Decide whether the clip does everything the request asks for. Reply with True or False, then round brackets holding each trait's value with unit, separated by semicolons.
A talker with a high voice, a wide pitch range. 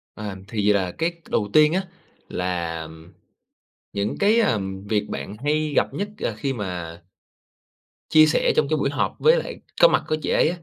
False (115 Hz; 8.2 semitones)